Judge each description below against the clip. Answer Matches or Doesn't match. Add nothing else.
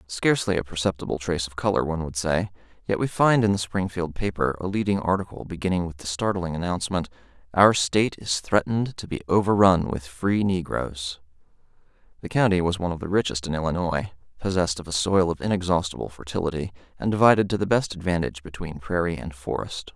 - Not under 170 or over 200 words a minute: Matches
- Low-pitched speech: Matches